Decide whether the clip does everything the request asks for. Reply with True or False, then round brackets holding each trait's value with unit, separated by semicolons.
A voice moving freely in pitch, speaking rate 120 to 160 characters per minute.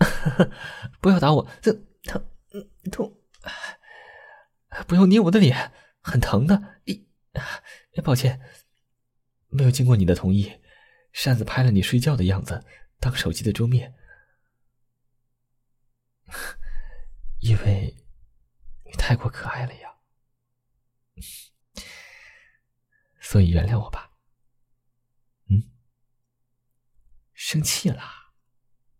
False (1.6 semitones; 135 characters per minute)